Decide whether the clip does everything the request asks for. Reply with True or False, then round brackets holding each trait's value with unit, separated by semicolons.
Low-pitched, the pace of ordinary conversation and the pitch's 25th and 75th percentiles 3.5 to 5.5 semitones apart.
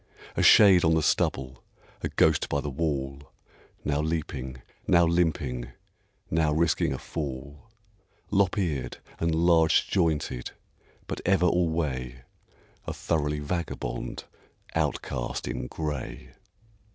False (75 Hz; 115 wpm; 3.9 semitones)